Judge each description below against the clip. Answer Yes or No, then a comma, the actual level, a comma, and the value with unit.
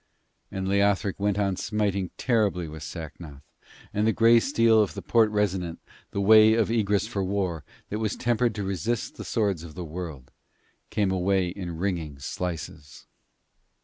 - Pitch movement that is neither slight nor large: Yes, average, 3.5 semitones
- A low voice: Yes, low, 100 Hz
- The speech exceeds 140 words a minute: Yes, average, 160 wpm